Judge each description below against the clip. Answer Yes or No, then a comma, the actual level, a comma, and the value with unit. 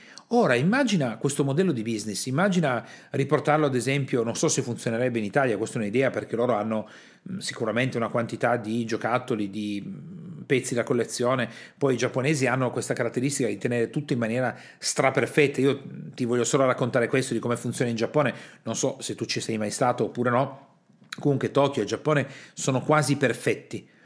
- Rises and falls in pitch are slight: No, average, 3.7 semitones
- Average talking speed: No, fast, 175 wpm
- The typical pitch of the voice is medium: No, low, 130 Hz